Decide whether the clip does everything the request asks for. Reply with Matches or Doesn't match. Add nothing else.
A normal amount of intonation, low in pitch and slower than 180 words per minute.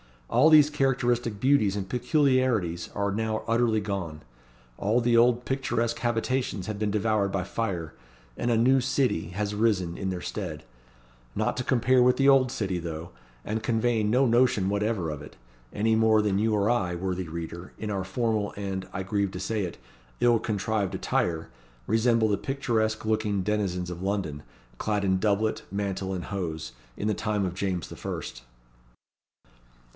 Matches